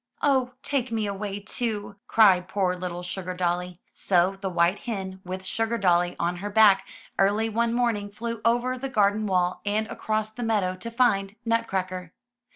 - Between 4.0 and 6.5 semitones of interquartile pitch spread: No, average, 3.6 semitones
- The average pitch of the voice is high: Yes, high, 205 Hz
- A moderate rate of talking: Yes, average, 160 wpm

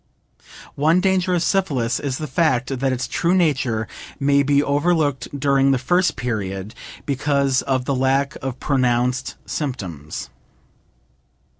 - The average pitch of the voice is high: No, low, 135 Hz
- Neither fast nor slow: No, slow, 130 wpm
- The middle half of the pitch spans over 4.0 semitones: No, average, 3.0 semitones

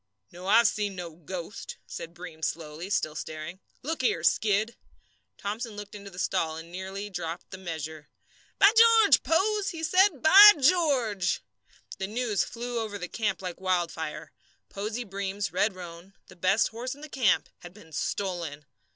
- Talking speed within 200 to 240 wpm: No, average, 160 wpm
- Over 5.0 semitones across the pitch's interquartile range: Yes, wide, 5.4 semitones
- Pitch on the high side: Yes, high, 195 Hz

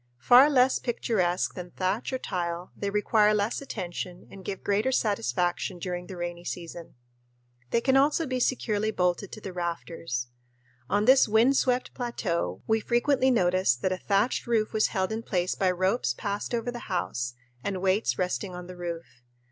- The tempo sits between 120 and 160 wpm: No, average, 170 wpm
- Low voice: No, high, 195 Hz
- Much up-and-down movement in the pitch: No, average, 4.6 semitones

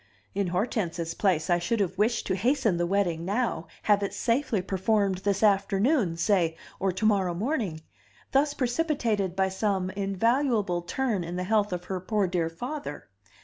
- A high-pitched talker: Yes, high, 195 Hz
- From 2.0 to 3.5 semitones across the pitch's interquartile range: No, average, 3.9 semitones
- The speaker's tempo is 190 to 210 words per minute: No, average, 165 wpm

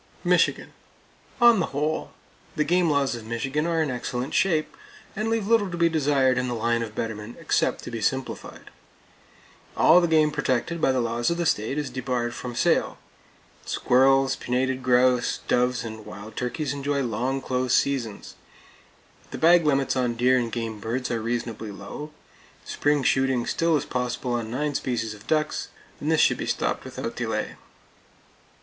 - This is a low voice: Yes, low, 130 Hz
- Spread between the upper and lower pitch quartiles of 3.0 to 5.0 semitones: Yes, average, 4.0 semitones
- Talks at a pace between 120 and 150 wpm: No, average, 170 wpm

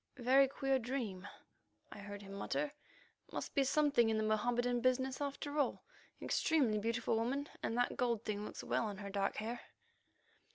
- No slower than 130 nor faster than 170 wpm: Yes, average, 165 wpm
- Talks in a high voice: Yes, high, 240 Hz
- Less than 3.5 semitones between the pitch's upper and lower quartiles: No, average, 4.0 semitones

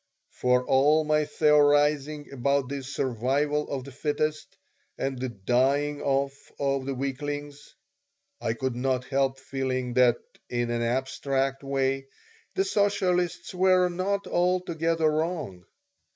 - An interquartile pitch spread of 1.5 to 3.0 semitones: Yes, narrow, 2.6 semitones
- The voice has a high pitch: No, medium, 140 Hz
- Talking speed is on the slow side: Yes, slow, 125 wpm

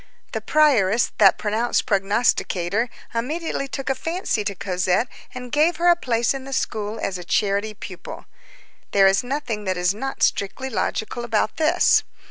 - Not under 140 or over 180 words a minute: Yes, average, 160 wpm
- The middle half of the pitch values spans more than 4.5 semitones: Yes, average, 5.1 semitones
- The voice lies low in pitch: No, high, 225 Hz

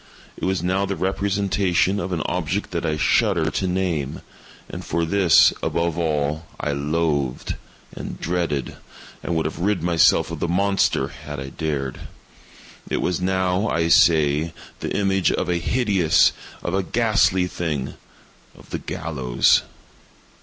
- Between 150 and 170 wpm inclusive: No, slow, 135 wpm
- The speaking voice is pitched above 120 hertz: No, very low, 85 Hz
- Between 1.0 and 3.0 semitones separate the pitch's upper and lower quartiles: No, average, 3.6 semitones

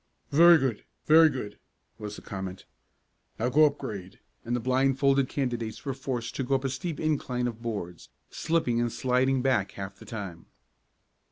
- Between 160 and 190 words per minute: Yes, average, 170 wpm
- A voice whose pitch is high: No, low, 125 Hz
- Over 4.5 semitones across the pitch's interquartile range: No, average, 3.7 semitones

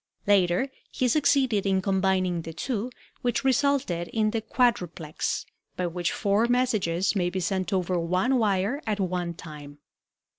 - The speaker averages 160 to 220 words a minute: No, average, 145 wpm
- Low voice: No, high, 190 Hz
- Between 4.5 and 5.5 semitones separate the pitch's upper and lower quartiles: Yes, average, 5.0 semitones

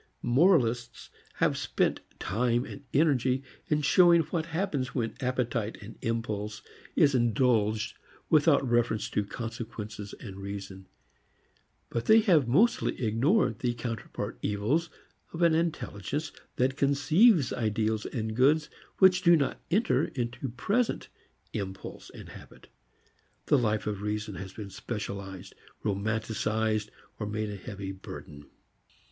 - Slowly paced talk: Yes, slow, 120 wpm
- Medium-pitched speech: No, low, 120 Hz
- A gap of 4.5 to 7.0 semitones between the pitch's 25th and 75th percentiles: Yes, wide, 5.5 semitones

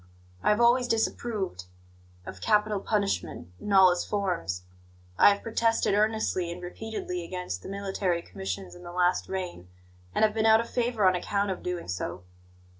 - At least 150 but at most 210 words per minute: Yes, average, 170 wpm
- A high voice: Yes, high, 195 Hz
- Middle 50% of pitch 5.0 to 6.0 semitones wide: No, average, 3.5 semitones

